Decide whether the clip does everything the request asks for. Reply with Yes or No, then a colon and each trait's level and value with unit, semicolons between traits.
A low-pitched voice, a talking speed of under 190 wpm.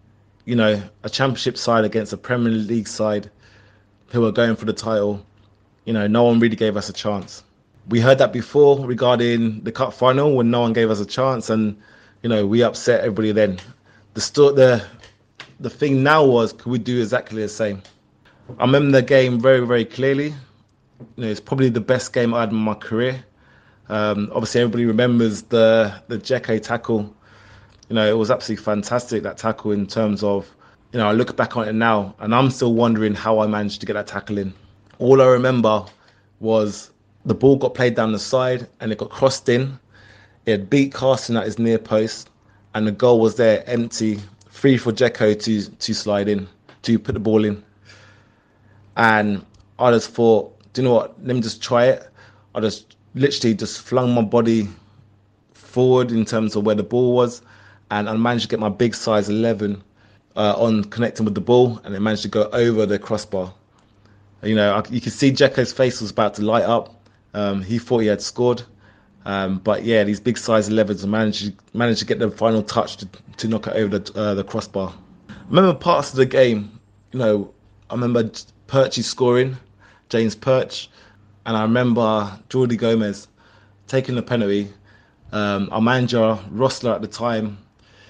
No: low, 110 Hz; average, 195 wpm